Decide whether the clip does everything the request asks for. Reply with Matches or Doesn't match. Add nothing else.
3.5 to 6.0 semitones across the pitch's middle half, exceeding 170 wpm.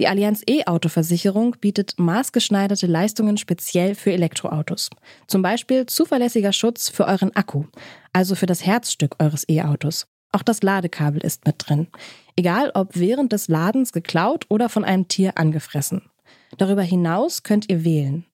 Doesn't match